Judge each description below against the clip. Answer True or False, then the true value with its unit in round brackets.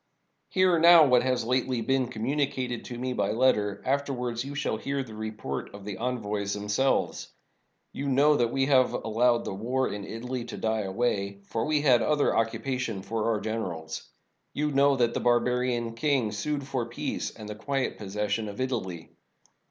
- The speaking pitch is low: True (120 Hz)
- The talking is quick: False (185 wpm)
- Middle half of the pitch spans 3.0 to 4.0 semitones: True (3.7 semitones)